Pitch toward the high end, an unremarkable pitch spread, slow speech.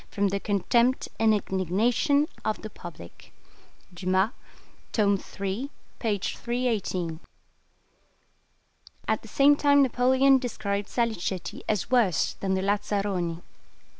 Yes: high, 205 Hz; average, 4.5 semitones; slow, 105 wpm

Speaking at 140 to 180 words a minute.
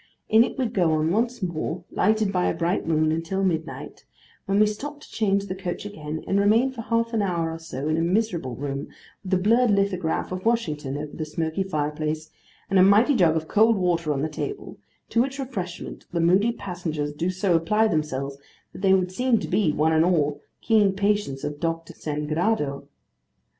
No: average, 200 wpm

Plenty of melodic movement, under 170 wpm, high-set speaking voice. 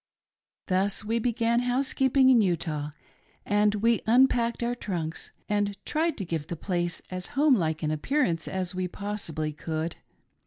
Yes: wide, 5.9 semitones; average, 155 wpm; high, 205 Hz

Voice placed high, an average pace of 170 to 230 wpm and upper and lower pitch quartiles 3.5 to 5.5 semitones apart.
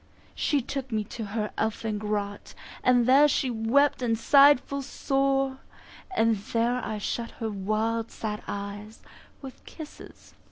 No: high, 230 Hz; average, 150 wpm; average, 4.0 semitones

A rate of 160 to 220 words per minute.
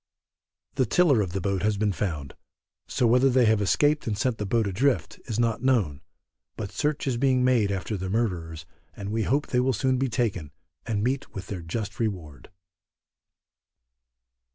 Yes: average, 175 wpm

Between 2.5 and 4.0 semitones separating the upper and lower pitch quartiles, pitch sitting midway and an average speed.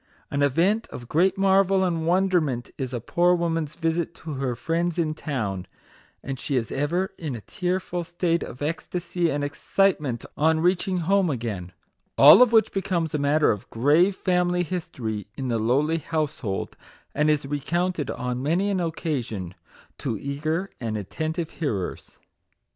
No: average, 4.9 semitones; medium, 160 Hz; average, 160 wpm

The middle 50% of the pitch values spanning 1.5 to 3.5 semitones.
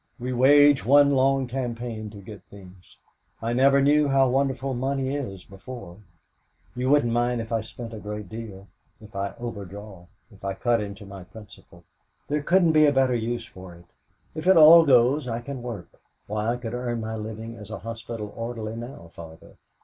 No: average, 4.2 semitones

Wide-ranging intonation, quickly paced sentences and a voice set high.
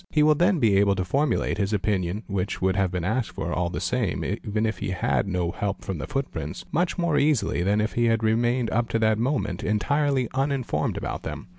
No: wide, 5.8 semitones; fast, 230 wpm; low, 110 Hz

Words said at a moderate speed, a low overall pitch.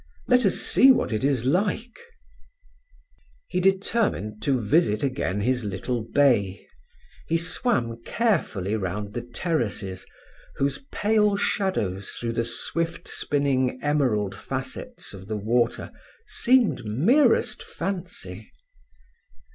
No: slow, 110 wpm; low, 130 Hz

